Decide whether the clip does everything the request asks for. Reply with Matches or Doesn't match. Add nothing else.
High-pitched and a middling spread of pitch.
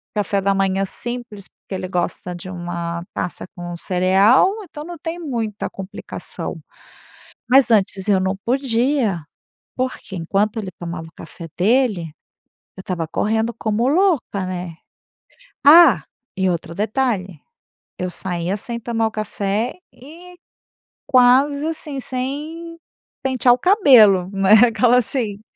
Doesn't match